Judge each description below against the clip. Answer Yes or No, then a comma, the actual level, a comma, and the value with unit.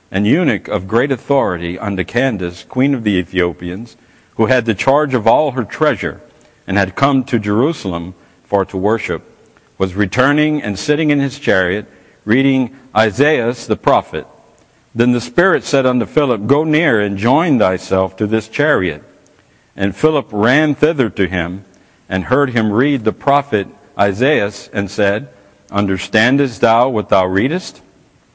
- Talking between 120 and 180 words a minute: Yes, average, 150 wpm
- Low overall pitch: Yes, low, 115 Hz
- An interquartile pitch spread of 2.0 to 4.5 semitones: No, wide, 5.4 semitones